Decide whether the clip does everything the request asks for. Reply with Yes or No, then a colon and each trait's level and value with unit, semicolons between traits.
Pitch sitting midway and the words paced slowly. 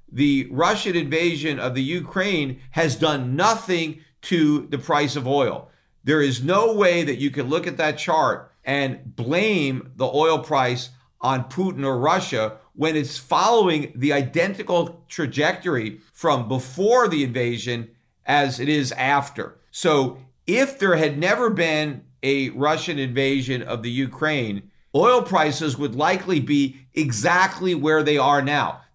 No: medium, 145 Hz; average, 145 wpm